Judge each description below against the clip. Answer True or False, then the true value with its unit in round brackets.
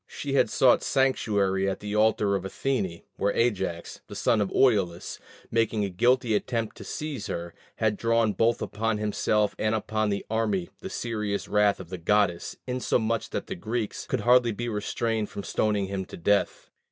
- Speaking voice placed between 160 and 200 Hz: False (105 Hz)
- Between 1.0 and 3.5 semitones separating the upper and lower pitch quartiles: True (2.6 semitones)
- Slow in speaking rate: False (175 wpm)